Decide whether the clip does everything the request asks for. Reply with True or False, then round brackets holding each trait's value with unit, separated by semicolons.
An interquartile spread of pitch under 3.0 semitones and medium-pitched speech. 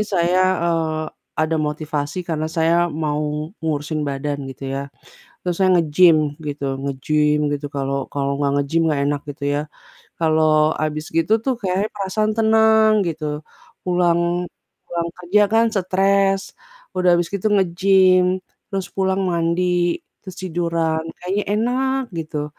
False (3.8 semitones; 170 Hz)